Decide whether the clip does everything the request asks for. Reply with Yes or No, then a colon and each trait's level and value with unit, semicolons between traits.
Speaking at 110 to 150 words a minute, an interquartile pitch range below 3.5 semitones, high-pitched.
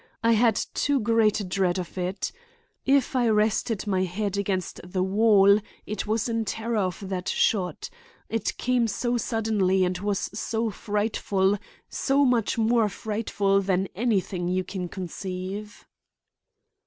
Yes: average, 140 wpm; average, 3.1 semitones; high, 205 Hz